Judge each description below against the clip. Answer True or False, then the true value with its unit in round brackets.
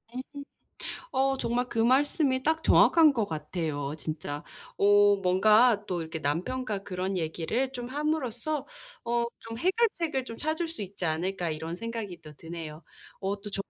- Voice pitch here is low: False (210 Hz)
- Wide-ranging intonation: True (7.2 semitones)